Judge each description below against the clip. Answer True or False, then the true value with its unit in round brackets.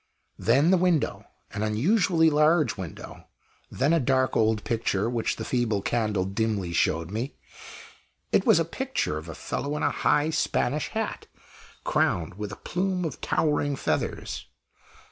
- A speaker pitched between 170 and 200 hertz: False (120 Hz)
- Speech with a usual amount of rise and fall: False (6.8 semitones)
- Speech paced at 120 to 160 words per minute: True (150 wpm)